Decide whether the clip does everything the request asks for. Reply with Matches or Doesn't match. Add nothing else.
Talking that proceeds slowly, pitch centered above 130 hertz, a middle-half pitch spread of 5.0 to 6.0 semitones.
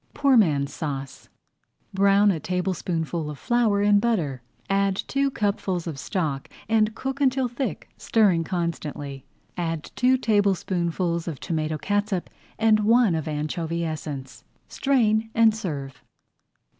Matches